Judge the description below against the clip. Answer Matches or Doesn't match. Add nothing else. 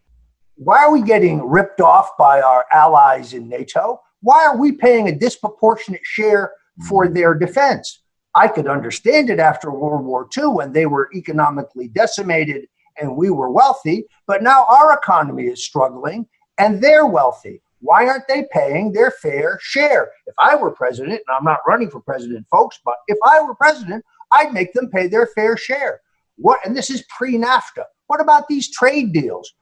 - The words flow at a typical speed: Matches